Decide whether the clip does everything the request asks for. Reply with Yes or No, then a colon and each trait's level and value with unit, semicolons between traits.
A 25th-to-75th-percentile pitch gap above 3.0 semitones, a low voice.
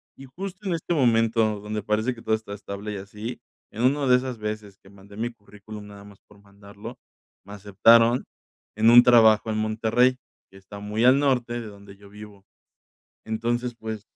No: average, 2.7 semitones; low, 110 Hz